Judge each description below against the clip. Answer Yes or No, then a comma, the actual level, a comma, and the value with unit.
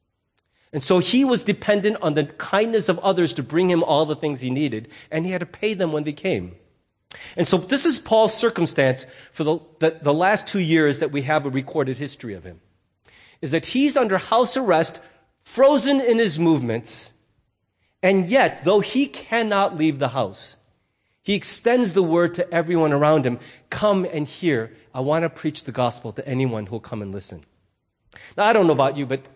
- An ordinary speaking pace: Yes, average, 195 wpm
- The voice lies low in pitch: No, medium, 155 Hz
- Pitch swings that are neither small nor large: No, wide, 7.0 semitones